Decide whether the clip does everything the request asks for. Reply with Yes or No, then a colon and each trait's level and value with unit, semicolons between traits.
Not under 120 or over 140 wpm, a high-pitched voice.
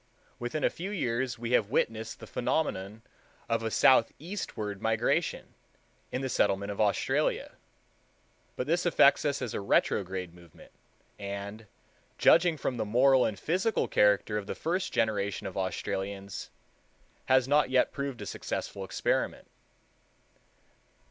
No: slow, 135 wpm; low, 115 Hz